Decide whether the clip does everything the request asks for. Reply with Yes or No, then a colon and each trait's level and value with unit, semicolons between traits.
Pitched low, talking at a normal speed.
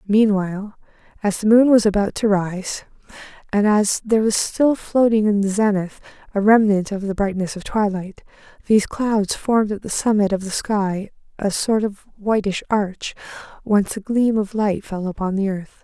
No: high, 205 Hz; average, 180 wpm